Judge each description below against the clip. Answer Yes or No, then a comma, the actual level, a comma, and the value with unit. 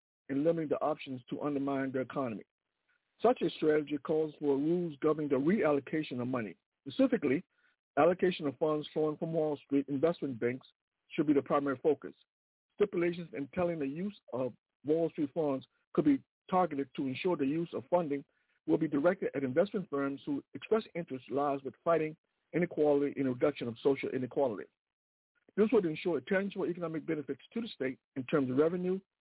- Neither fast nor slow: Yes, average, 175 wpm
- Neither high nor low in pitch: Yes, medium, 155 Hz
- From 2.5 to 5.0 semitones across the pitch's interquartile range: Yes, average, 3.9 semitones